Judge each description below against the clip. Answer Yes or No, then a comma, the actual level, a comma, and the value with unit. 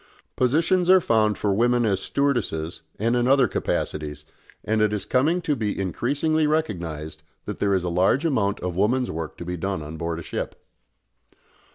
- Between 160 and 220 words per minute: Yes, average, 180 wpm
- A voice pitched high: No, low, 105 Hz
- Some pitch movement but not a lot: No, wide, 7.3 semitones